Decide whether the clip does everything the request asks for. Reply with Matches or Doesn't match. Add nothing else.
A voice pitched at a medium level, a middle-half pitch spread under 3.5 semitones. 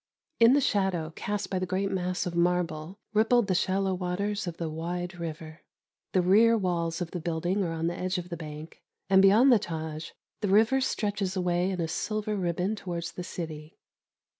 Matches